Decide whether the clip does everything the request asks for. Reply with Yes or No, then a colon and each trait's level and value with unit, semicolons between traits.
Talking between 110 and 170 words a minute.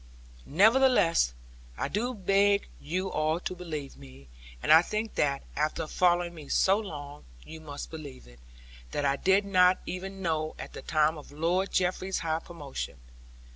Yes: average, 165 wpm